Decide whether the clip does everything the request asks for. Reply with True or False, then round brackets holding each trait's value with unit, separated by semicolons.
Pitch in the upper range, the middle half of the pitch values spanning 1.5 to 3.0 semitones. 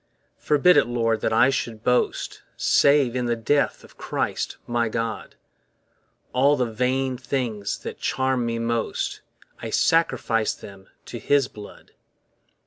False (120 Hz; 2.7 semitones)